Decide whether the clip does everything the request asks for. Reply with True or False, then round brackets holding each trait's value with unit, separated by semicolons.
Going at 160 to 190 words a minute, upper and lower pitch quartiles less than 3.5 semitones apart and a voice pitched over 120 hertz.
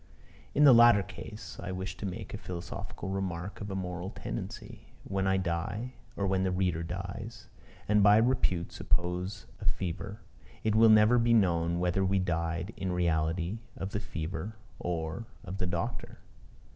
False (165 wpm; 3.0 semitones; 95 Hz)